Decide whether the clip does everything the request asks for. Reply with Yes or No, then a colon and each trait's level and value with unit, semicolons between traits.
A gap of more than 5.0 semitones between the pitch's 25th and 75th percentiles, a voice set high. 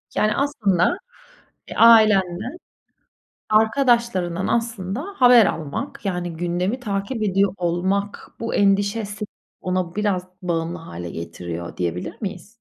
No: average, 4.0 semitones; high, 195 Hz